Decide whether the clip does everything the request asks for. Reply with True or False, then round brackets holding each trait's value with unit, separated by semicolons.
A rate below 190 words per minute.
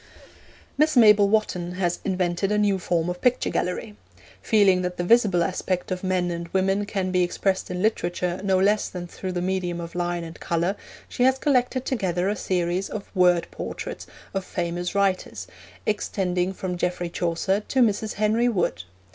True (170 wpm)